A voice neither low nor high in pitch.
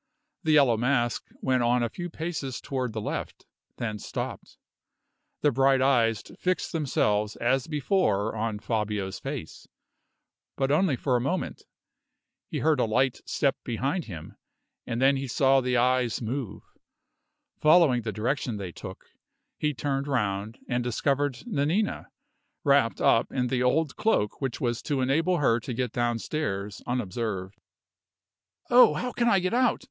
No: low, 130 Hz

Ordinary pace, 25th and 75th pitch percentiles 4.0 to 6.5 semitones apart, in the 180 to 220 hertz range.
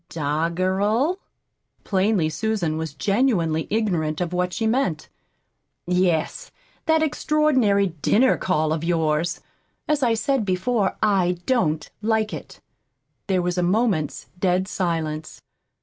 No: slow, 120 wpm; average, 5.2 semitones; medium, 185 Hz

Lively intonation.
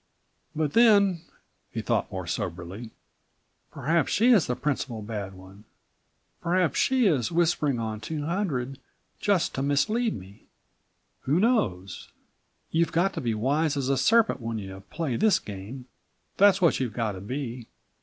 Yes: wide, 8.0 semitones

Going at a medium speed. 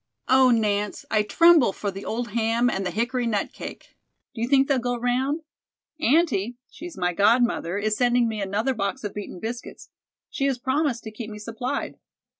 Yes: average, 185 wpm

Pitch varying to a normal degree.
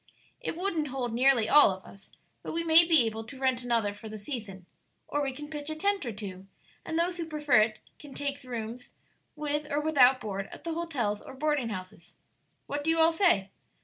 No: wide, 5.9 semitones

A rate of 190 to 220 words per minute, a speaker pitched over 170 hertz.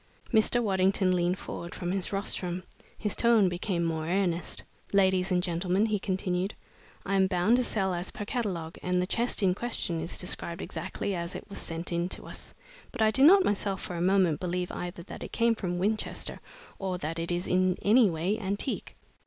Yes: average, 195 wpm; medium, 185 Hz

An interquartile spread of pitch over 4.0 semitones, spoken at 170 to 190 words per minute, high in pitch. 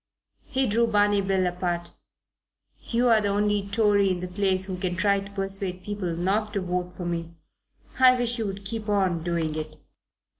No: narrow, 2.6 semitones; average, 180 wpm; high, 195 Hz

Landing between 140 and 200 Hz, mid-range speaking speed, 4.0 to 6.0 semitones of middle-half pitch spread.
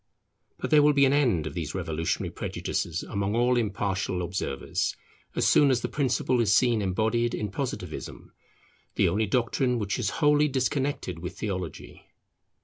No: low, 110 Hz; average, 155 wpm; wide, 5.6 semitones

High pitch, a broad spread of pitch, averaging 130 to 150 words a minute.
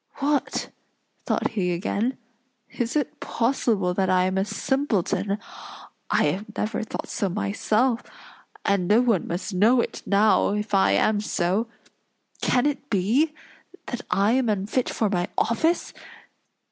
No: high, 210 Hz; average, 4.1 semitones; average, 140 wpm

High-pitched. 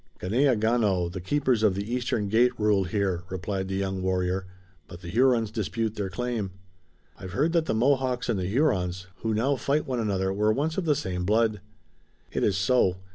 No: low, 105 Hz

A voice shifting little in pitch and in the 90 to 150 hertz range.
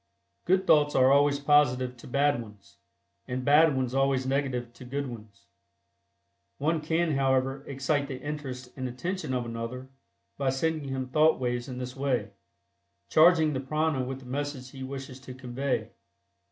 Yes: narrow, 2.3 semitones; low, 135 Hz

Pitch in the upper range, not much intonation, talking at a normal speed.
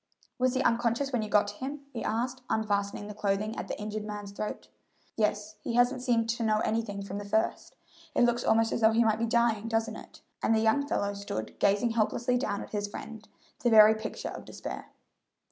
No: high, 220 Hz; narrow, 2.2 semitones; fast, 215 wpm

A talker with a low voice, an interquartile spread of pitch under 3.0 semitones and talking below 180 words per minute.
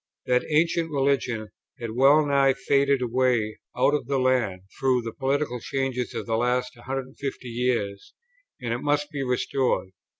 Yes: low, 130 Hz; narrow, 2.5 semitones; average, 155 wpm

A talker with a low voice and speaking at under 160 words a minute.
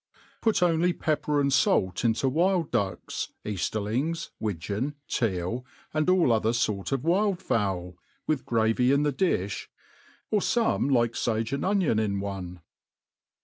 Yes: low, 125 Hz; average, 145 wpm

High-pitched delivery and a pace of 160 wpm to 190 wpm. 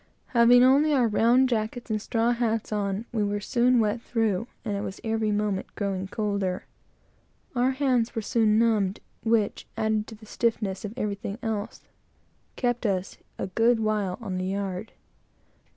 Yes: high, 220 Hz; average, 170 wpm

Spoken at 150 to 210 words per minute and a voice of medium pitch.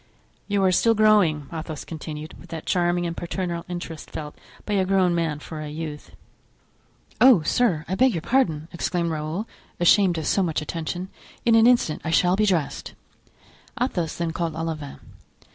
Yes: average, 170 wpm; medium, 170 Hz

